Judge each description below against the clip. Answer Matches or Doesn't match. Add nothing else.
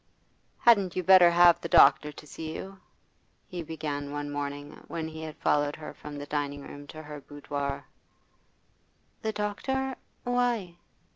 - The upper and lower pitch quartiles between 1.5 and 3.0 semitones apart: Doesn't match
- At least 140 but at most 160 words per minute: Matches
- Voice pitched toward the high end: Doesn't match